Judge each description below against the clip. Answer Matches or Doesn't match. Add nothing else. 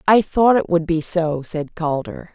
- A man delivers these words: Doesn't match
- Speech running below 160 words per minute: Doesn't match